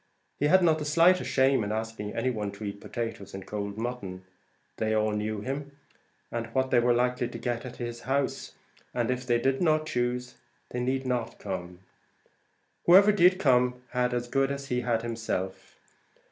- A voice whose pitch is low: Yes, low, 125 Hz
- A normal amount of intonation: Yes, average, 3.4 semitones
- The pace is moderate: Yes, average, 185 wpm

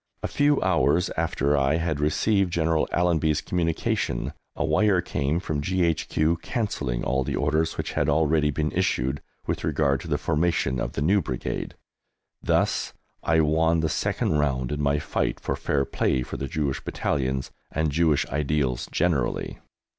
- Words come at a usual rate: Yes, average, 160 wpm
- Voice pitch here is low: Yes, very low, 75 Hz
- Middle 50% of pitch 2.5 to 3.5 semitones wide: Yes, average, 3.0 semitones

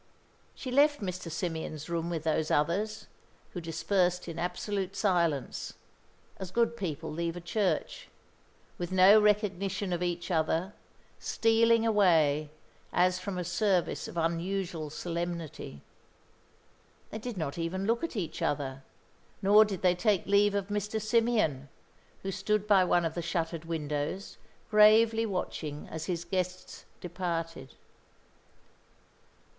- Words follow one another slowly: Yes, slow, 130 wpm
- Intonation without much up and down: No, average, 3.7 semitones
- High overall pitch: No, medium, 180 Hz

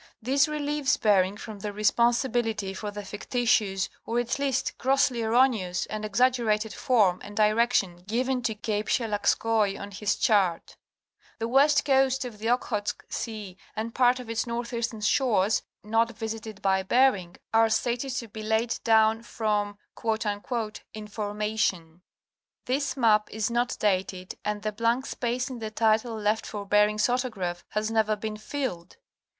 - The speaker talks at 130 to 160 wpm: Yes, average, 145 wpm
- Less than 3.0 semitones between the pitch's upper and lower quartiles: Yes, narrow, 2.6 semitones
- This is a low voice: No, high, 220 Hz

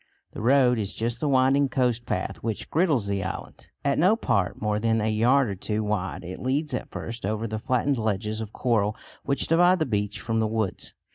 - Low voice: Yes, low, 115 Hz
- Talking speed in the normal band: No, fast, 210 wpm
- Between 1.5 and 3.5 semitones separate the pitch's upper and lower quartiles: No, average, 3.9 semitones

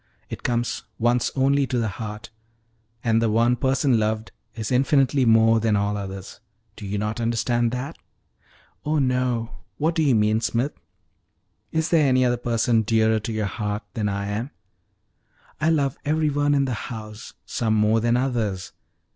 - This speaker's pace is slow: No, average, 165 wpm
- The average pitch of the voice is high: No, low, 115 Hz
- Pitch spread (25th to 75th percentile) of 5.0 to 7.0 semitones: No, average, 3.3 semitones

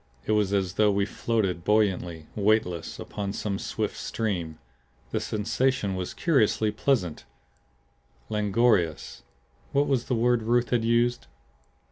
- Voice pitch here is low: Yes, low, 105 Hz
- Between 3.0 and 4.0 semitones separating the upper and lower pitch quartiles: Yes, average, 3.5 semitones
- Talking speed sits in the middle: No, slow, 125 wpm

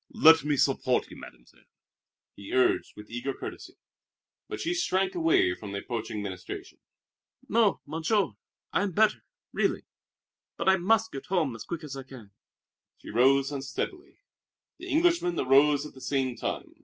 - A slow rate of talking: No, average, 155 wpm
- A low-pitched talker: No, medium, 145 Hz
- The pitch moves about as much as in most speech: No, wide, 7.0 semitones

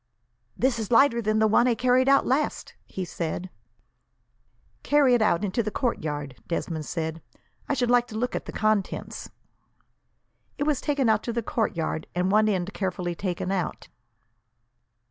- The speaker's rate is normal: Yes, average, 165 wpm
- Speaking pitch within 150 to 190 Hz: No, high, 215 Hz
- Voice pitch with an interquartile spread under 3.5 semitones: No, wide, 5.5 semitones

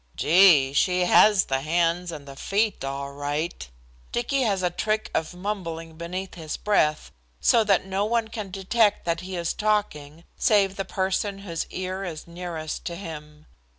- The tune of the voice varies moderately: Yes, average, 3.9 semitones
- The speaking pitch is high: No, medium, 180 Hz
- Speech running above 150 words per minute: Yes, average, 165 wpm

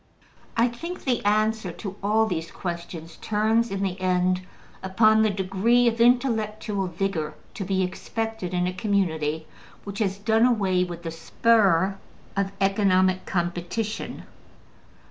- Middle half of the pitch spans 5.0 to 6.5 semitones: No, average, 3.4 semitones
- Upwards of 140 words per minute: No, slow, 135 wpm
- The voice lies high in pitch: Yes, high, 195 Hz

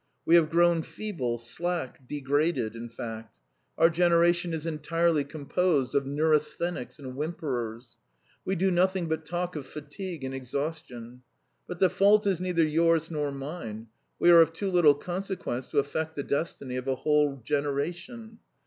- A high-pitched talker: No, medium, 155 Hz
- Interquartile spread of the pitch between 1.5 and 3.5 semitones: No, average, 4.1 semitones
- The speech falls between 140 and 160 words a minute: Yes, average, 155 wpm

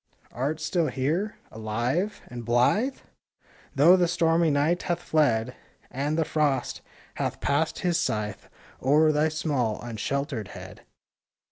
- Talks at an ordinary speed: No, slow, 125 wpm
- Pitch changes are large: No, average, 5.0 semitones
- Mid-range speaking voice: Yes, medium, 150 Hz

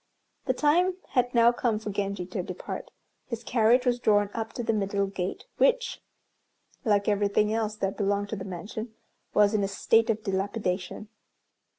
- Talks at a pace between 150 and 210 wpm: Yes, average, 170 wpm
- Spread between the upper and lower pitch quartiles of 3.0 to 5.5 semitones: No, narrow, 2.6 semitones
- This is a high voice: Yes, high, 210 Hz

